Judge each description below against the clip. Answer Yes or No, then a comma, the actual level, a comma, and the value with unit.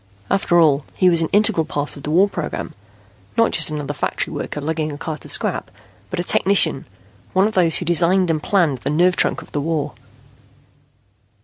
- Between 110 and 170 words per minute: No, average, 195 wpm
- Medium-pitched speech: Yes, medium, 165 Hz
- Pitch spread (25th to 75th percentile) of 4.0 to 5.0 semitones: No, average, 3.4 semitones